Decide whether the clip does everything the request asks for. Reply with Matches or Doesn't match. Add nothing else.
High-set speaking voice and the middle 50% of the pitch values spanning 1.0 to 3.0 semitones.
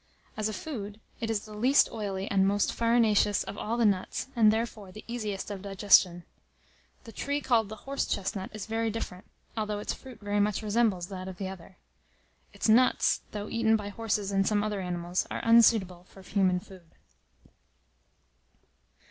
Matches